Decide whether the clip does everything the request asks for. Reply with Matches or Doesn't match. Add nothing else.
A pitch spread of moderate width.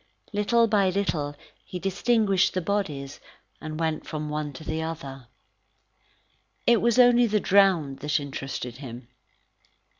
Doesn't match